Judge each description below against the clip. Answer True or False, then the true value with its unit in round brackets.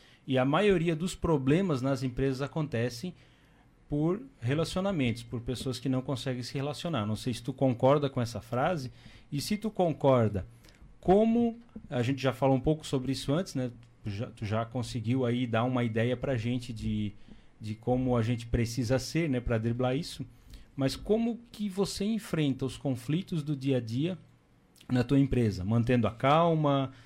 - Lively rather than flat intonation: False (4.0 semitones)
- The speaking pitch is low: True (130 Hz)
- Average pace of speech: True (175 wpm)